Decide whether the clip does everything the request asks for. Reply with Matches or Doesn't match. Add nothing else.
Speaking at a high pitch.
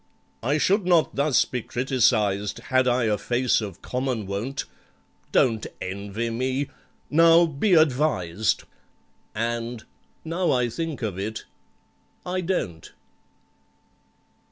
Doesn't match